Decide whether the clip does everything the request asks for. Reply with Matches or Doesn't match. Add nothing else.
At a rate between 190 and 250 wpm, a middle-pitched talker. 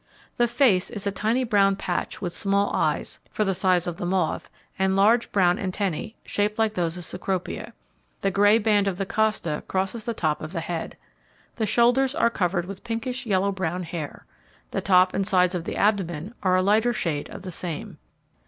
Doesn't match